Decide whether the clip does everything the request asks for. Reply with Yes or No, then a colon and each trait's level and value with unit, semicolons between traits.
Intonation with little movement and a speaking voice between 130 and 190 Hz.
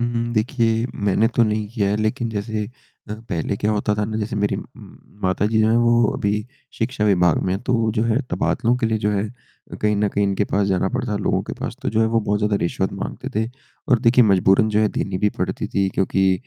No: narrow, 1.9 semitones; low, 105 Hz